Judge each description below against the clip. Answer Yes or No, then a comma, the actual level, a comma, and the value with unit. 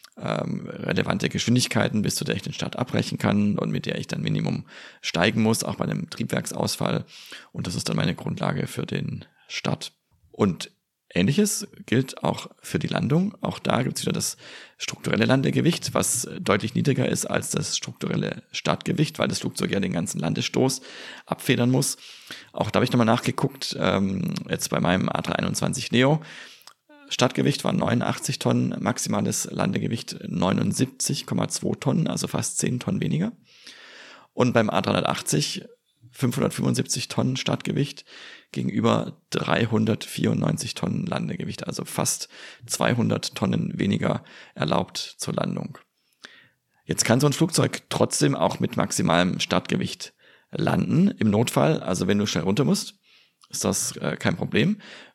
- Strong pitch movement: Yes, wide, 8.2 semitones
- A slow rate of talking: No, average, 140 wpm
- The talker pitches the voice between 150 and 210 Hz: No, medium, 140 Hz